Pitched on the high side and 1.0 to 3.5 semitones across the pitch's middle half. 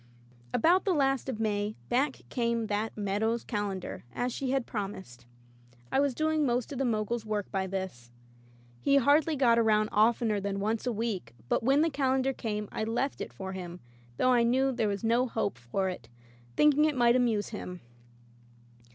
No: high, 230 Hz; average, 4.3 semitones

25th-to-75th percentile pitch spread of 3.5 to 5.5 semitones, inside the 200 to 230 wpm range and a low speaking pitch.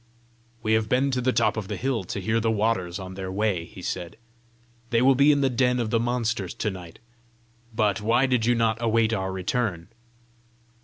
Yes: average, 4.2 semitones; fast, 205 wpm; low, 110 Hz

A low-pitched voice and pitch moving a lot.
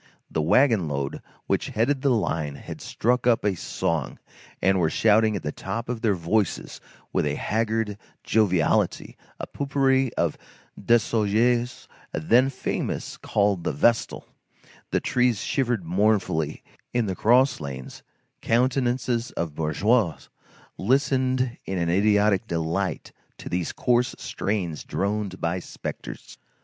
Yes: low, 105 Hz; wide, 5.7 semitones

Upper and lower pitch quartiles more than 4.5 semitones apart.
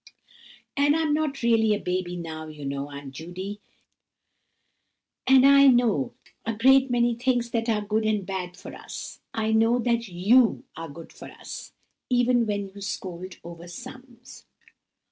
Yes: wide, 5.5 semitones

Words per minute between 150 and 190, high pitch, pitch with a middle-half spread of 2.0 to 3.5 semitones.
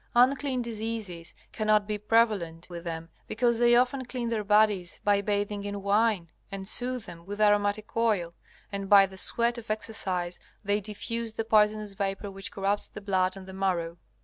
Yes: average, 175 wpm; high, 205 Hz; average, 2.7 semitones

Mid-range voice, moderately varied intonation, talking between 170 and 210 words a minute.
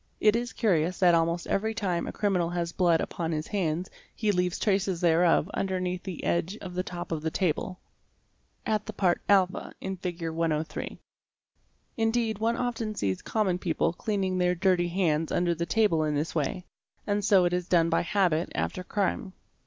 Yes: medium, 180 Hz; average, 3.1 semitones; average, 180 wpm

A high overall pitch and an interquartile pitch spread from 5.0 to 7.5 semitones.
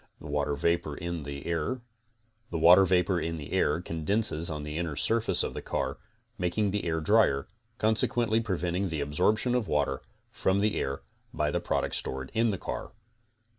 No: very low, 85 Hz; wide, 5.6 semitones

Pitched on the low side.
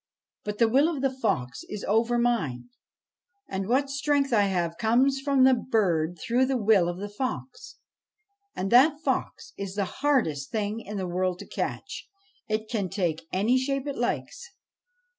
No: high, 225 Hz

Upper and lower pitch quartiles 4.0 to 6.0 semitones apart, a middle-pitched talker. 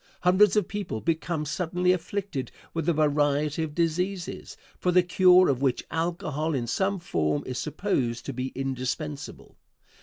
Yes: average, 4.5 semitones; medium, 160 Hz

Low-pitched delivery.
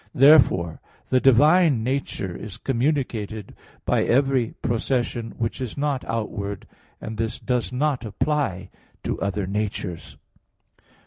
Yes: low, 115 Hz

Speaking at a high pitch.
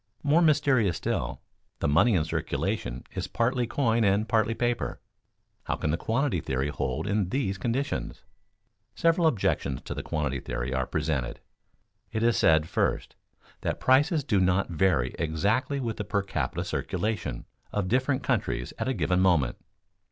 No: low, 105 Hz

